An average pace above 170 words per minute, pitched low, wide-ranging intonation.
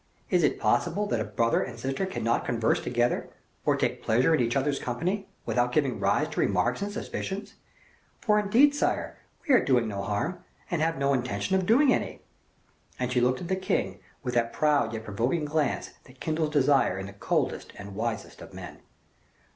Yes: average, 190 wpm; low, 130 Hz; wide, 7.0 semitones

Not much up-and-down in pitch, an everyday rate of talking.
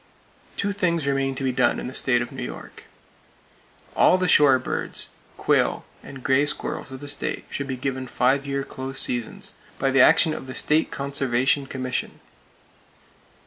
Yes: narrow, 1.5 semitones; average, 170 wpm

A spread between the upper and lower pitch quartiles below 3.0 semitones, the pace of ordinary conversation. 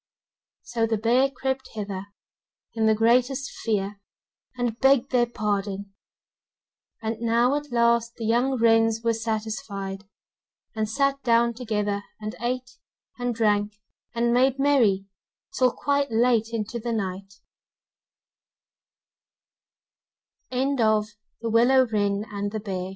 No: narrow, 2.6 semitones; slow, 100 wpm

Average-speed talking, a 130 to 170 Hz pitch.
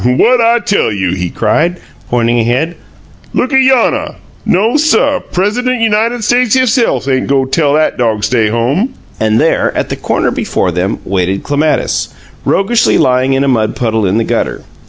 Yes: average, 165 wpm; medium, 140 Hz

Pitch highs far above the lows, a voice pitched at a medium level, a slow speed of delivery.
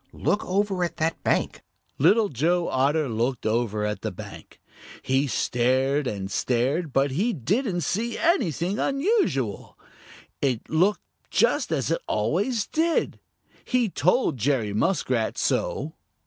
Yes: wide, 8.4 semitones; medium, 155 Hz; slow, 130 wpm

